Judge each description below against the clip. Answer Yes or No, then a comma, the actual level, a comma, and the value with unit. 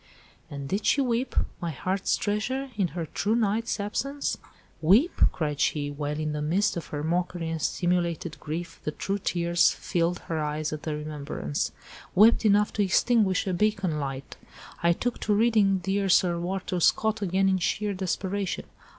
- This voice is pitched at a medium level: Yes, medium, 180 Hz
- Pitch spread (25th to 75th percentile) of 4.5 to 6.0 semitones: Yes, average, 4.8 semitones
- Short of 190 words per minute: Yes, average, 160 wpm